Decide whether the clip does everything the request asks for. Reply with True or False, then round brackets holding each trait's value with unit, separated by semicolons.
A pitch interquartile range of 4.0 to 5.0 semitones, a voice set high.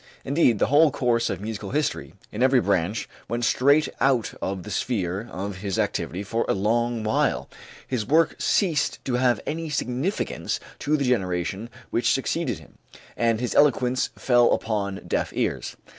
False (4.6 semitones; 120 Hz)